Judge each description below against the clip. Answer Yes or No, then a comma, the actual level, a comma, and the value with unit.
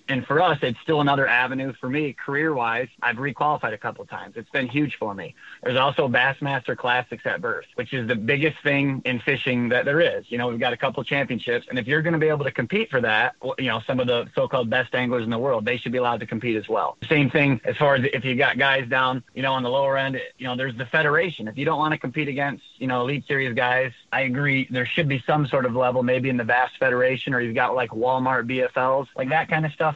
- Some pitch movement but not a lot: No, narrow, 2.3 semitones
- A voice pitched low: Yes, low, 130 Hz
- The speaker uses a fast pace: Yes, fast, 260 wpm